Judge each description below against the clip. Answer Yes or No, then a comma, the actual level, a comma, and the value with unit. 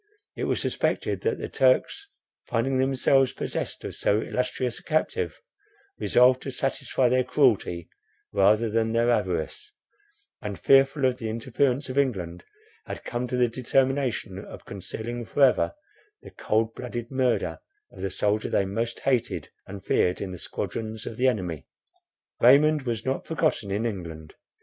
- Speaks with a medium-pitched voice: No, low, 120 Hz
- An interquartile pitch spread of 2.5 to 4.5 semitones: Yes, average, 4.0 semitones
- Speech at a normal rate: Yes, average, 155 wpm